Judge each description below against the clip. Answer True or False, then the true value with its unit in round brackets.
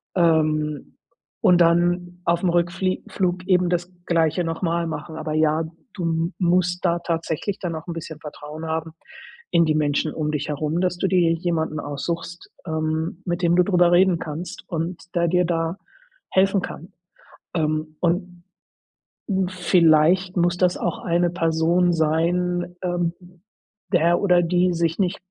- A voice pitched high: False (170 Hz)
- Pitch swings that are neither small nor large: False (1.8 semitones)